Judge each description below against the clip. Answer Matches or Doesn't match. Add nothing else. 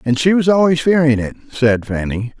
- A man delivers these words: Matches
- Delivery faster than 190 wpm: Matches